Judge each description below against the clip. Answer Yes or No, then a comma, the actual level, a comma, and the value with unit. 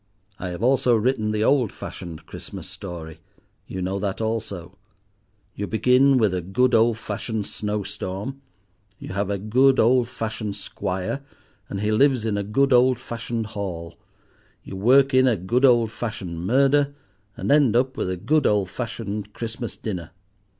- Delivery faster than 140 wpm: Yes, average, 155 wpm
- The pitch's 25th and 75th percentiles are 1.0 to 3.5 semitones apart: No, average, 4.5 semitones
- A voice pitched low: Yes, low, 110 Hz